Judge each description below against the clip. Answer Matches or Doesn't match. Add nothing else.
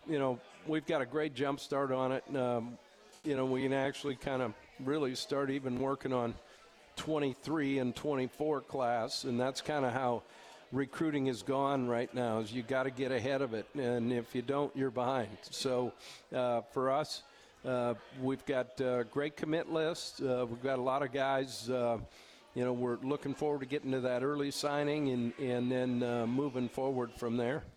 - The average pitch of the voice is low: Matches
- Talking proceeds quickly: Doesn't match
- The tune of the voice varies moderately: Doesn't match